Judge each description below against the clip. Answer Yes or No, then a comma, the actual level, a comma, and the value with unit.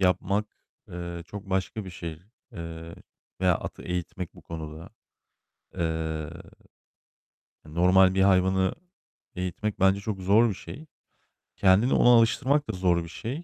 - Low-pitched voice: Yes, very low, 95 Hz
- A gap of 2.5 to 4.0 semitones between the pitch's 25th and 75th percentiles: Yes, average, 2.9 semitones